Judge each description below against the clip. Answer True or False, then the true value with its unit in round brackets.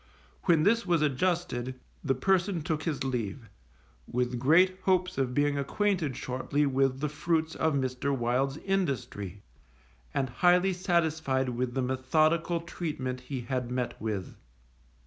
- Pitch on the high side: False (140 Hz)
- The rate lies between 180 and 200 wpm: False (135 wpm)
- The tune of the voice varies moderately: True (4.9 semitones)